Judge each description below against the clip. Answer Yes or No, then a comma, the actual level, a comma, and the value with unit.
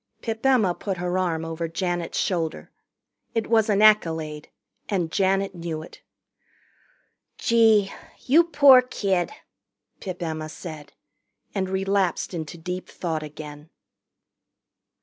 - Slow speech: Yes, slow, 115 wpm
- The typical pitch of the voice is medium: Yes, medium, 180 Hz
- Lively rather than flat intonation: No, average, 4.2 semitones